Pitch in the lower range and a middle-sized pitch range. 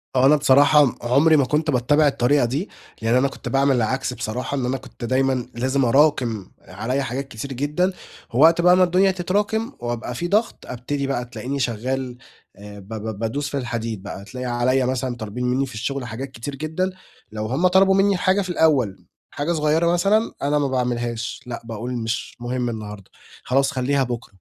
Yes: low, 130 Hz; average, 3.7 semitones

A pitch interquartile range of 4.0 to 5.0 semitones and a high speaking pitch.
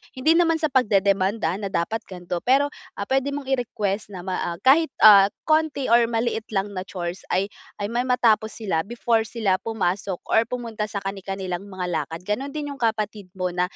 Yes: average, 4.4 semitones; high, 215 Hz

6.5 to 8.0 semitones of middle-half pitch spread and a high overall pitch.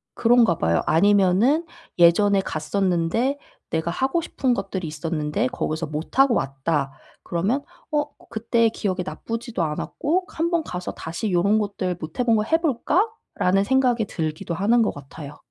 Yes: wide, 6.9 semitones; high, 200 Hz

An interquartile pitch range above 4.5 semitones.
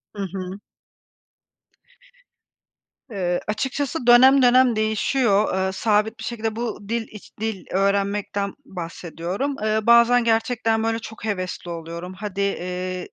No: average, 3.6 semitones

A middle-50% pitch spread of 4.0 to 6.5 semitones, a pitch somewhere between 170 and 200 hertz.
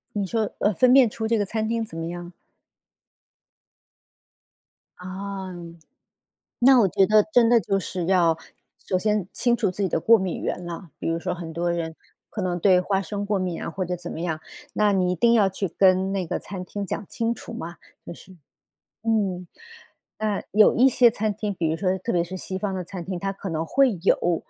No: average, 3.3 semitones; high, 190 Hz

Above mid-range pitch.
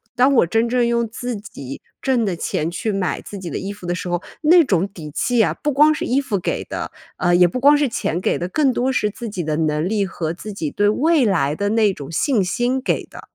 Yes: high, 205 Hz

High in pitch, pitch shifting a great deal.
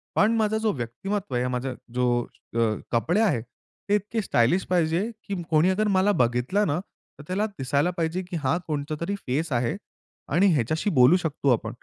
No: medium, 160 Hz; wide, 7.6 semitones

